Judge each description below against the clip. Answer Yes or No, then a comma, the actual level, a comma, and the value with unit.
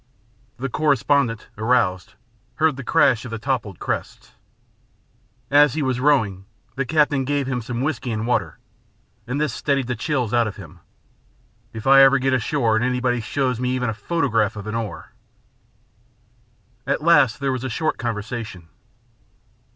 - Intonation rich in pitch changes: No, average, 3.4 semitones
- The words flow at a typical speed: Yes, average, 160 wpm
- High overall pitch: No, low, 125 Hz